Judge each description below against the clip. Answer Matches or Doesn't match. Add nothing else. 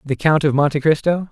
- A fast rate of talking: Matches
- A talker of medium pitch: Matches